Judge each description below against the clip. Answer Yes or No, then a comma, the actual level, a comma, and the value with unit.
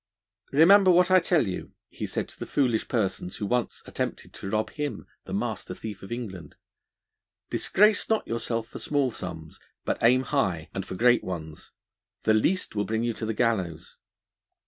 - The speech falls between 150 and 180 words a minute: Yes, average, 175 wpm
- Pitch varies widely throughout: Yes, wide, 6.7 semitones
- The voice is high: No, low, 115 Hz